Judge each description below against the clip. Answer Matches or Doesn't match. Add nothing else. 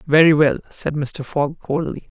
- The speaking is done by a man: Doesn't match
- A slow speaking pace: Doesn't match